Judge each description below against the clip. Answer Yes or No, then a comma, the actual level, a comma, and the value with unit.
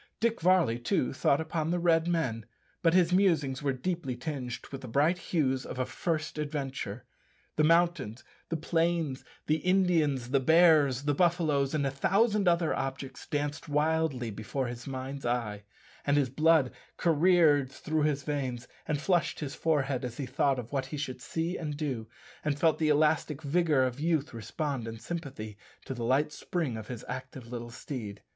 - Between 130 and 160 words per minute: No, average, 175 wpm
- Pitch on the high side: No, medium, 145 Hz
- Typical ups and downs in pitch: Yes, average, 3.9 semitones